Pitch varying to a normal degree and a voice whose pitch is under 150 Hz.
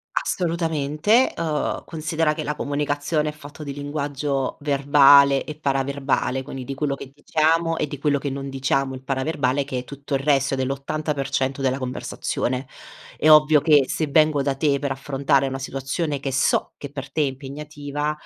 No: narrow, 1.8 semitones; medium, 140 Hz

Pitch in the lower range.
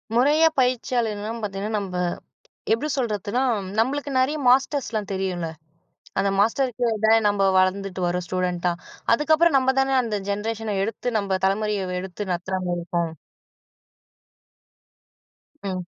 No: high, 210 Hz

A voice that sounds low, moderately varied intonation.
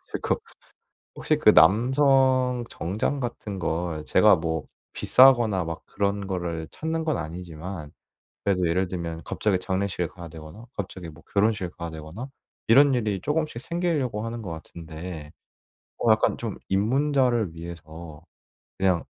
No: very low, 95 Hz; wide, 6.4 semitones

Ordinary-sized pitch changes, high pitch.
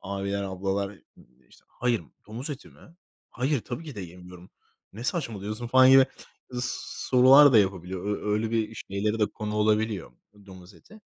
No: average, 4.0 semitones; low, 105 Hz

